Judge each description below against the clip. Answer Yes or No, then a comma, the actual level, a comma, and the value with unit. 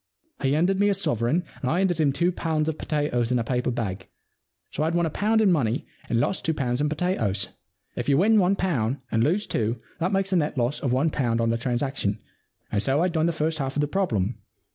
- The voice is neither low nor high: Yes, medium, 145 Hz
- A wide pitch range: Yes, wide, 6.3 semitones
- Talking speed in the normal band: No, fast, 240 wpm